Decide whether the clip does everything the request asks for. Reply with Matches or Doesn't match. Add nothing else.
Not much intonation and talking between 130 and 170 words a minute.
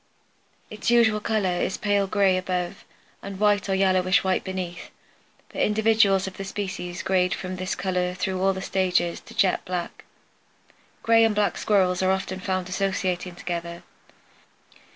Matches